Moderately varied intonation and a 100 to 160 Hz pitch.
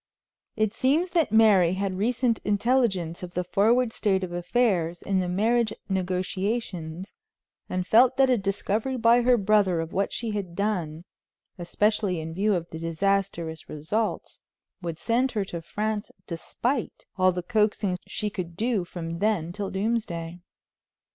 No: average, 4.2 semitones; high, 200 Hz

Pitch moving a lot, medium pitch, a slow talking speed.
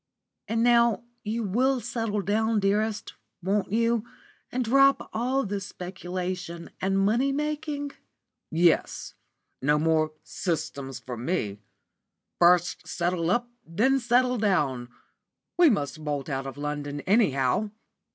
No: wide, 6.8 semitones; high, 195 Hz; slow, 120 wpm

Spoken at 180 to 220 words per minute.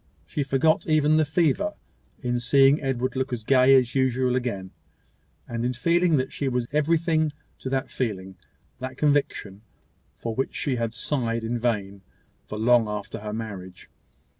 No: average, 160 wpm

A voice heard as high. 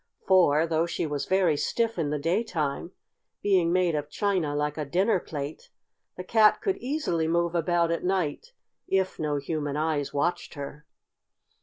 No: medium, 165 Hz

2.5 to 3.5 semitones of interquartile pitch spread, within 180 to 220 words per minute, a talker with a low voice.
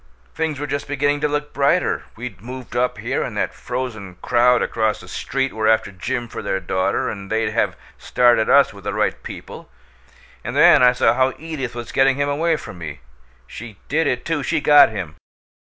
No: average, 4.6 semitones; average, 200 wpm; low, 125 Hz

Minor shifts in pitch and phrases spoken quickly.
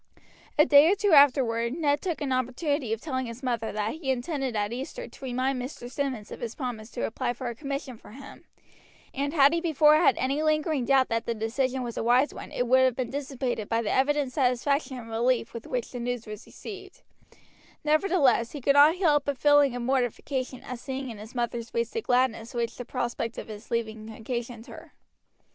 No: average, 3.4 semitones; fast, 210 wpm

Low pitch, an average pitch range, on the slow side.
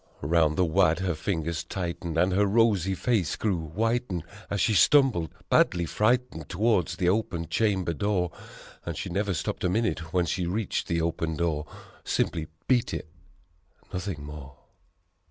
No: very low, 90 Hz; average, 3.8 semitones; average, 155 wpm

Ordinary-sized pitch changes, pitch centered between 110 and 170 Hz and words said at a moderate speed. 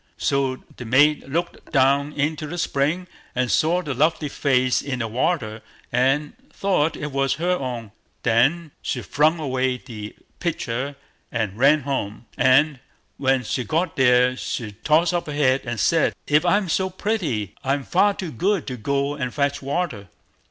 Yes: average, 3.9 semitones; medium, 140 Hz; average, 160 wpm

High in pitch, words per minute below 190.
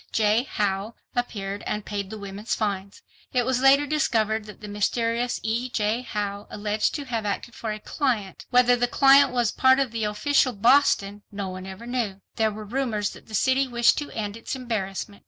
No: high, 220 Hz; average, 195 wpm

